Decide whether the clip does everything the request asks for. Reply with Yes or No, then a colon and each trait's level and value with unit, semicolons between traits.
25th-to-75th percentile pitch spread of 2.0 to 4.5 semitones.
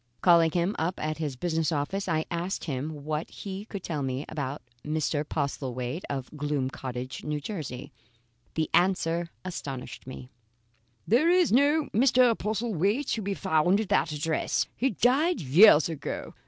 No: wide, 5.5 semitones